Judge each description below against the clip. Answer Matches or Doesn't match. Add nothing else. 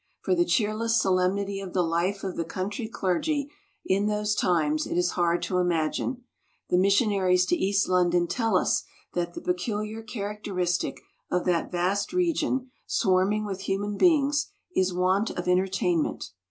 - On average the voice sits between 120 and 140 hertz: Doesn't match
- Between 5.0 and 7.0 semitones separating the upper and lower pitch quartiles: Doesn't match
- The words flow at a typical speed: Matches